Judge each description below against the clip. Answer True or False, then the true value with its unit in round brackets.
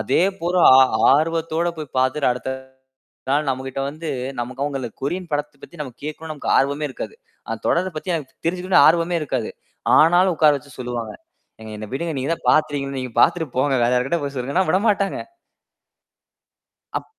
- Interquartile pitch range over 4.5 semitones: False (4.1 semitones)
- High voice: False (150 Hz)